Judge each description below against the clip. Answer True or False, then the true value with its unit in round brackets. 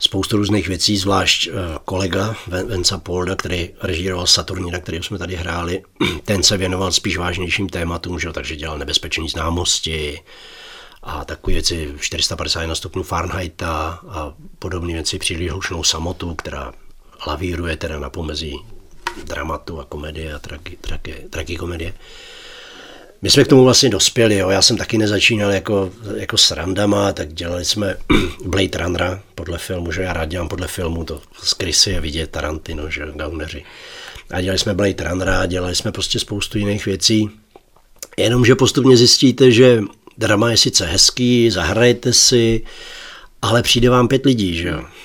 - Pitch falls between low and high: False (95 Hz)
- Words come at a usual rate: True (145 wpm)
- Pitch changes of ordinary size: True (3.5 semitones)